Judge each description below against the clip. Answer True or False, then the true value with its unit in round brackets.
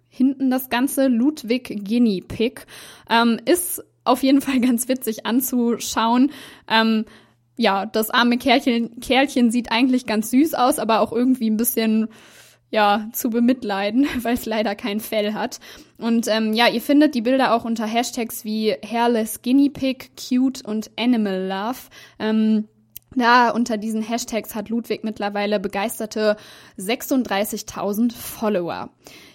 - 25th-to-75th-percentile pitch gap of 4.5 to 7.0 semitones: False (2.6 semitones)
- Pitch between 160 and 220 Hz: False (230 Hz)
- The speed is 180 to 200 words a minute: False (140 wpm)